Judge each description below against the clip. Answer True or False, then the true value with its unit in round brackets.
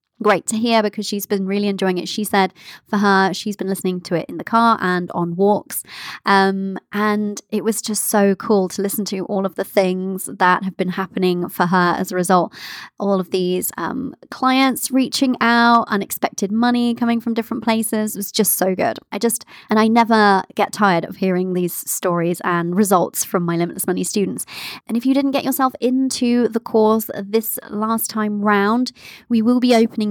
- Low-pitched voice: False (210 Hz)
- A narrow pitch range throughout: False (3.4 semitones)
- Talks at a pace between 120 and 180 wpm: False (200 wpm)